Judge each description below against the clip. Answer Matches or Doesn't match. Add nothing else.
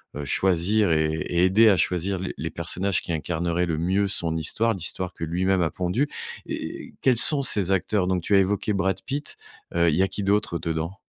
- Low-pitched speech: Matches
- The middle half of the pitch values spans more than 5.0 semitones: Doesn't match